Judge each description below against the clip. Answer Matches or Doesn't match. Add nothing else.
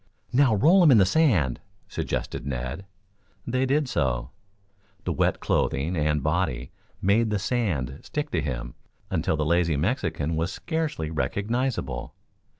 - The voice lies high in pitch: Doesn't match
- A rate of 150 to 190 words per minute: Doesn't match